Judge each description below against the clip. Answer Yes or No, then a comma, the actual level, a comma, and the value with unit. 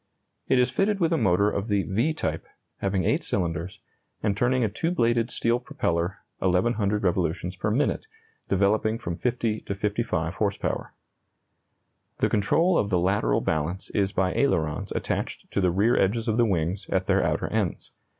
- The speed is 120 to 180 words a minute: Yes, average, 170 wpm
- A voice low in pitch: Yes, low, 100 Hz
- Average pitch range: Yes, average, 4.3 semitones